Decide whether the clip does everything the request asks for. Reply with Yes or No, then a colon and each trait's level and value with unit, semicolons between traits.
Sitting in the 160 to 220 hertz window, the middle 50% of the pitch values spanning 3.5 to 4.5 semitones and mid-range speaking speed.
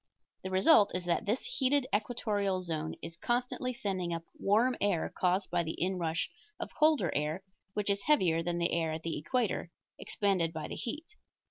No: high, 190 Hz; average, 5.1 semitones; average, 175 wpm